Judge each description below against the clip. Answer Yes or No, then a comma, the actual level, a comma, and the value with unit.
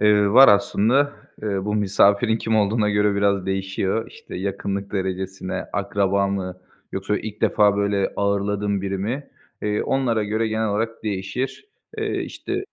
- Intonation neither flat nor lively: No, narrow, 1.8 semitones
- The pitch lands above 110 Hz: No, low, 100 Hz